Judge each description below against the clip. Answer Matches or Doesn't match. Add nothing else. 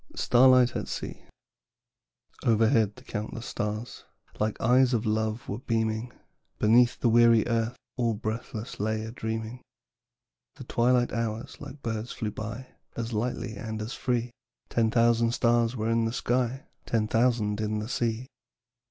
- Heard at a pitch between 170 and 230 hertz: Doesn't match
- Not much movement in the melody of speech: Matches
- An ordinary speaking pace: Matches